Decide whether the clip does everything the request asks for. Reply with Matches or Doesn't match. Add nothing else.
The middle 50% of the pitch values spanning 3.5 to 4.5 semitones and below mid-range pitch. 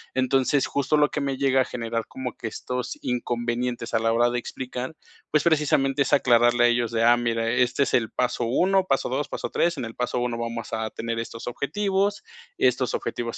Doesn't match